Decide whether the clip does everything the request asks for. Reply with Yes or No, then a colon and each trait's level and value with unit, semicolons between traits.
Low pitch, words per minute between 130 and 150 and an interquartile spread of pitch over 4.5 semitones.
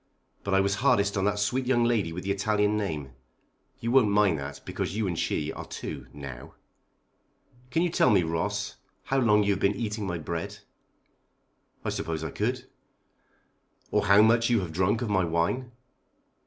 No: low, 100 Hz; average, 180 wpm; average, 4.9 semitones